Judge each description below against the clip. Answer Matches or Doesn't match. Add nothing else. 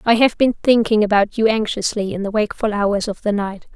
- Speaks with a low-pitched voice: Doesn't match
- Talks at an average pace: Doesn't match